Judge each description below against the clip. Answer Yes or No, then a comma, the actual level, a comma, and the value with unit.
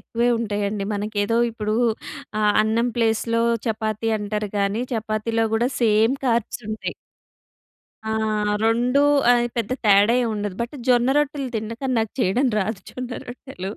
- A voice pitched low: No, high, 225 Hz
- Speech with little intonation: Yes, narrow, 2.2 semitones